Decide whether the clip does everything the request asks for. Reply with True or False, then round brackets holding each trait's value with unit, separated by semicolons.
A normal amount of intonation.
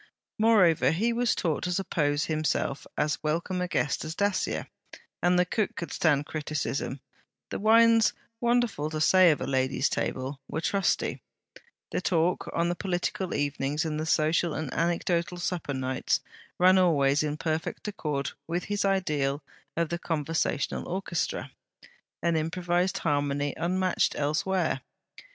True (3.8 semitones)